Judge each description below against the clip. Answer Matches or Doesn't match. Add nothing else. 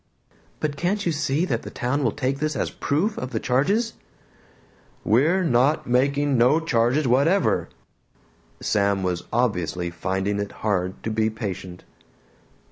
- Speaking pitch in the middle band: Doesn't match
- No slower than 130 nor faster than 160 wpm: Matches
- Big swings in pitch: Matches